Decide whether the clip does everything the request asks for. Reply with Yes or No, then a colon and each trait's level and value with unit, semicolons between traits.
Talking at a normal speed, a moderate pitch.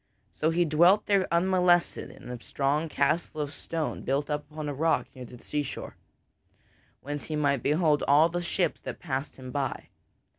Yes: average, 180 wpm; medium, 150 Hz